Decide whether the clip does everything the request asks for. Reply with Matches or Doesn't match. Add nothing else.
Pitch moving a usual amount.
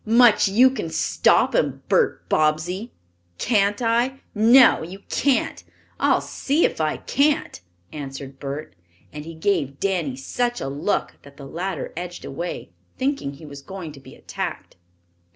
Doesn't match